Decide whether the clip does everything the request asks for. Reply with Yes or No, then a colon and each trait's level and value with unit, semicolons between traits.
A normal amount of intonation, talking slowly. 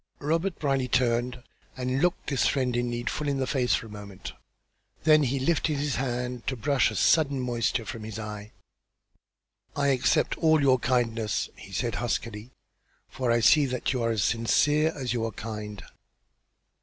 No: average, 3.4 semitones; average, 175 wpm